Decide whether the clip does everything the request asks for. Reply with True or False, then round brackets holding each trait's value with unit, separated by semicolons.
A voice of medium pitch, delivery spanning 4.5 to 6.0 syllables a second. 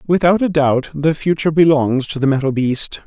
True (150 Hz; 5.2 syllables/s)